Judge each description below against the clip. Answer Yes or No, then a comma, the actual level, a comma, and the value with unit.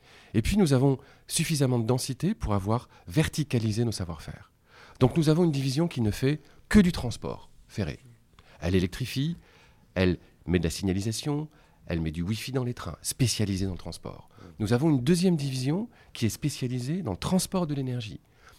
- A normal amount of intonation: No, wide, 6.8 semitones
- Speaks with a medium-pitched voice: No, low, 125 Hz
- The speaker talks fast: No, average, 180 wpm